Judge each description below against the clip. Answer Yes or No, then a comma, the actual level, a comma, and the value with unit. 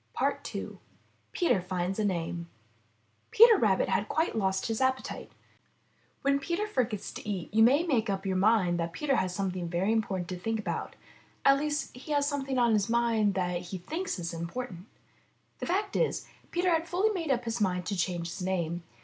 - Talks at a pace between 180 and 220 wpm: Yes, average, 185 wpm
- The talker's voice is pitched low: No, high, 215 Hz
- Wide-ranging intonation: Yes, wide, 7.2 semitones